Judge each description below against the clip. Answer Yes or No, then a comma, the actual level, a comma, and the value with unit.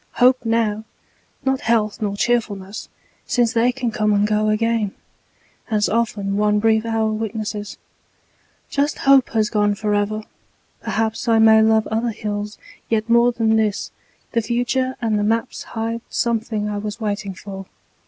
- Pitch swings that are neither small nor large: No, narrow, 1.8 semitones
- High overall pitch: Yes, high, 220 Hz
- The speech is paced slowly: No, average, 150 wpm